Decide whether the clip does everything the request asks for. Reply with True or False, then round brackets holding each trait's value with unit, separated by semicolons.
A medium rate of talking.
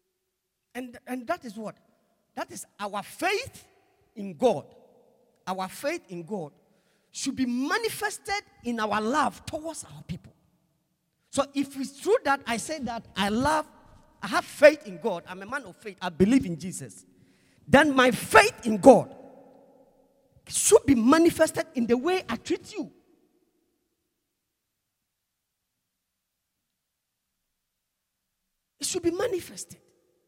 False (130 wpm)